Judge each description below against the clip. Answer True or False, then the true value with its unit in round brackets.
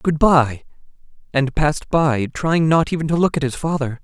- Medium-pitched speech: True (150 Hz)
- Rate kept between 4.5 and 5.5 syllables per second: True (5.1 syllables/s)